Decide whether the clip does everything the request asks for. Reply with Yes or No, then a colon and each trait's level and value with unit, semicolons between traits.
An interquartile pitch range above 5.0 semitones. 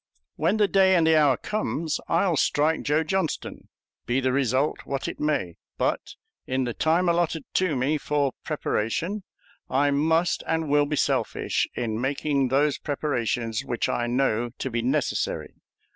No: average, 3.8 semitones